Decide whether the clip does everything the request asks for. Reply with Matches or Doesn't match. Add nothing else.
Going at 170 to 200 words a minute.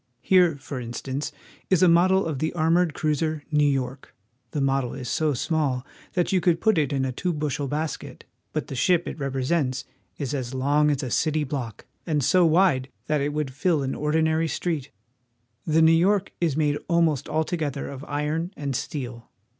Matches